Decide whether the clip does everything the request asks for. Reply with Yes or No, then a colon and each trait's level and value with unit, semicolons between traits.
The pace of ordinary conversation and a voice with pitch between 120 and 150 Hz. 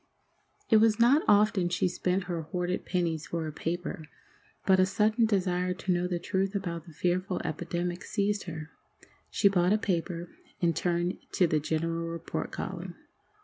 No: average, 165 wpm; medium, 180 Hz